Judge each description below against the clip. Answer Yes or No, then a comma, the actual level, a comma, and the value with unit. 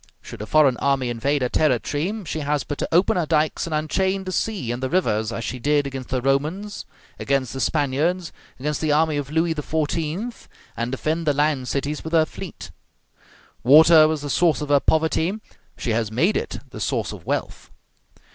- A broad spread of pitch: No, average, 3.3 semitones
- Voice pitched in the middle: Yes, medium, 150 Hz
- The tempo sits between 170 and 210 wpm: Yes, average, 195 wpm